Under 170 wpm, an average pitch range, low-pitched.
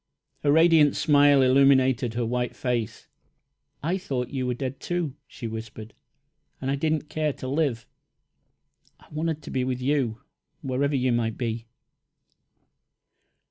Yes: average, 140 wpm; average, 3.2 semitones; low, 130 Hz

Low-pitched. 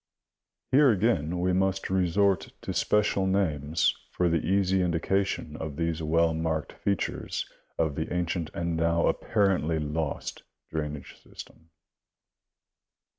Yes: very low, 85 Hz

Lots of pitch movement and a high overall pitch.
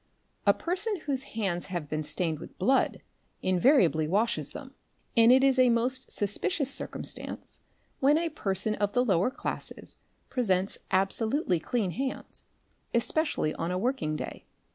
Yes: wide, 6.5 semitones; high, 225 Hz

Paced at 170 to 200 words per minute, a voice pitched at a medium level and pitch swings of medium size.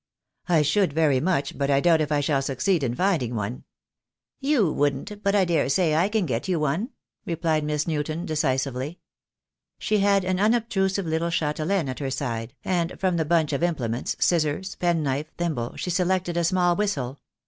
Yes: average, 175 wpm; medium, 160 Hz; average, 4.6 semitones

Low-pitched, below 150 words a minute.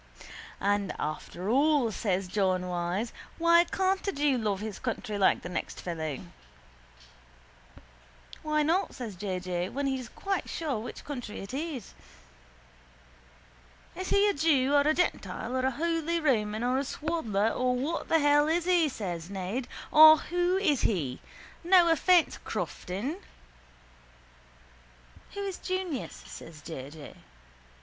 No: very high, 250 Hz; average, 140 wpm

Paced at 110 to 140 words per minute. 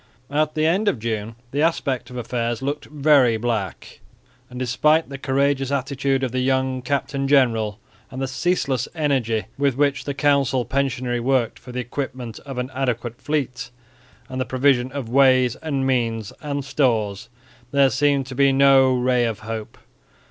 No: average, 165 wpm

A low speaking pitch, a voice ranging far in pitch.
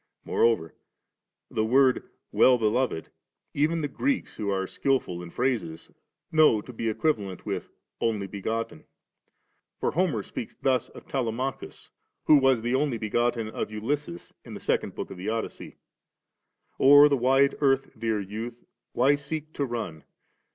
No: low, 120 Hz; average, 4.3 semitones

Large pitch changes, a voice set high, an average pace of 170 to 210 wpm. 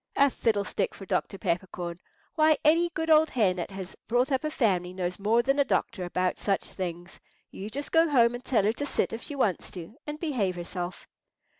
Yes: wide, 7.5 semitones; high, 215 Hz; fast, 205 wpm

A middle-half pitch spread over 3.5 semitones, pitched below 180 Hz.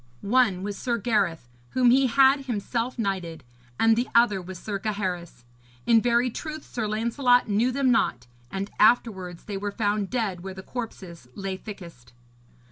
No: average, 4.2 semitones; high, 215 Hz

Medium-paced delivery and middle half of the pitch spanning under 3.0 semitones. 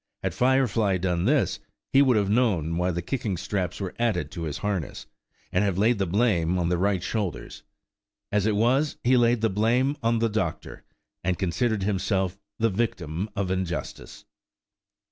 No: average, 170 wpm; average, 4.3 semitones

